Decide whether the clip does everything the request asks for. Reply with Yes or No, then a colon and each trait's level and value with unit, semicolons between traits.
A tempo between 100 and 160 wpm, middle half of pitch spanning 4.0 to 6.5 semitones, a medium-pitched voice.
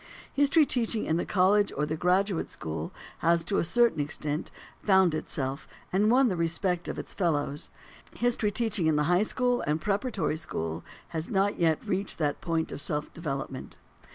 No: average, 175 wpm; average, 5.1 semitones; medium, 175 Hz